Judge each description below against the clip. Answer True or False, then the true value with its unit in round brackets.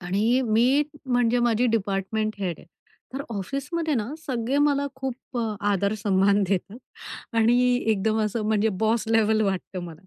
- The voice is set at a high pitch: True (220 Hz)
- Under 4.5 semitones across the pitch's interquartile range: True (3.7 semitones)